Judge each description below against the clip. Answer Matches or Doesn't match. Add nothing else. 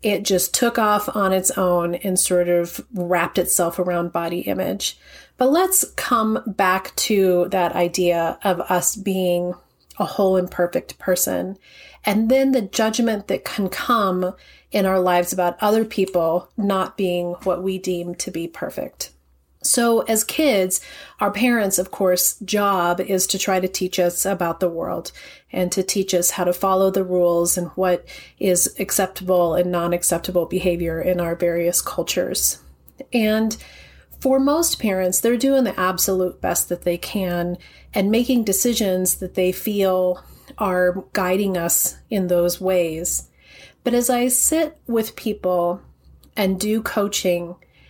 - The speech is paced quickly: Doesn't match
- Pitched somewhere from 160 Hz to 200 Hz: Matches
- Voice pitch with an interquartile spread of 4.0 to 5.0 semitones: Doesn't match